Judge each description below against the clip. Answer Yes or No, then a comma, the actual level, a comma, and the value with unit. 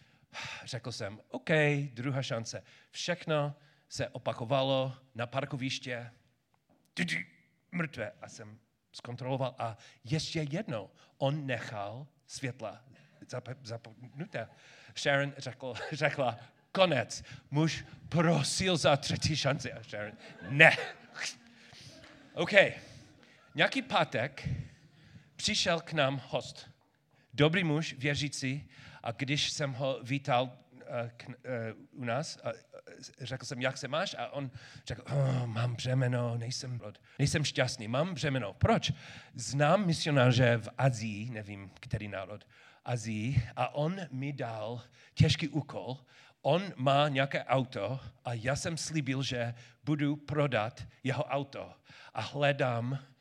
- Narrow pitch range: No, average, 3.2 semitones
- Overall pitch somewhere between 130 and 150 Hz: Yes, low, 135 Hz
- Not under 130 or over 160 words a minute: No, slow, 115 wpm